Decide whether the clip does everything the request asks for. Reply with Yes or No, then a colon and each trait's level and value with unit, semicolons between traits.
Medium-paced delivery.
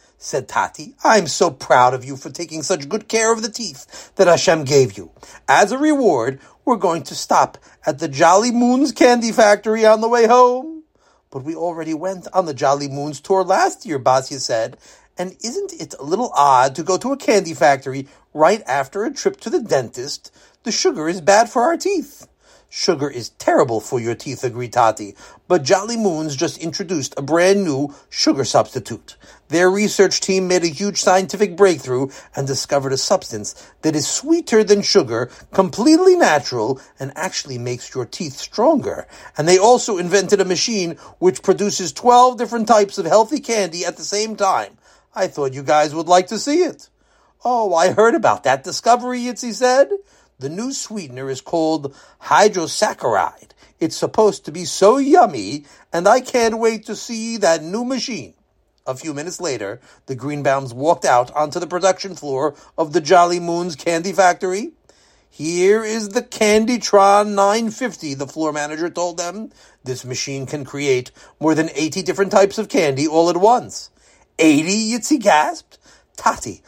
Yes: average, 170 wpm